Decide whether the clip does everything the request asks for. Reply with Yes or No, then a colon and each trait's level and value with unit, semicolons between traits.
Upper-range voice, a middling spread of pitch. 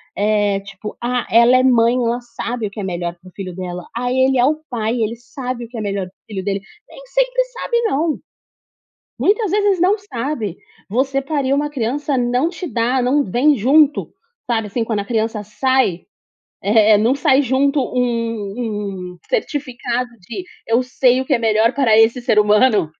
Yes: high, 240 Hz; average, 4.2 semitones